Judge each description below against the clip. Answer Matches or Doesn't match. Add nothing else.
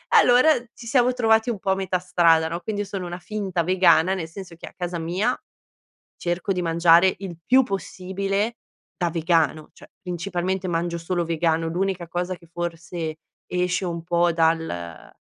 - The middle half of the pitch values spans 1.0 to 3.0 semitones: Matches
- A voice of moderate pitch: Matches